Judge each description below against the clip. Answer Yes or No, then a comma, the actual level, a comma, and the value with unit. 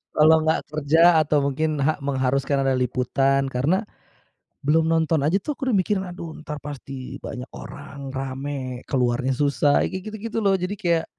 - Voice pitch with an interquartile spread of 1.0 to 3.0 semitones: No, average, 3.6 semitones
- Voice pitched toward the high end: No, medium, 145 Hz